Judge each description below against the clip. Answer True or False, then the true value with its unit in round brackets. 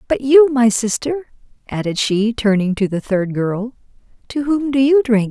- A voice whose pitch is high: True (235 Hz)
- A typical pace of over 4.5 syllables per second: False (4.4 syllables/s)